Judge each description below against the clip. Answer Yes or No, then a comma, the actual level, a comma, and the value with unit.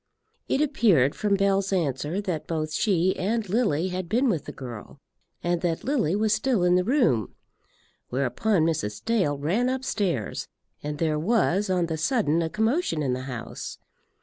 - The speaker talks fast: No, average, 165 wpm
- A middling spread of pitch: No, wide, 6.1 semitones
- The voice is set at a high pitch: No, medium, 180 Hz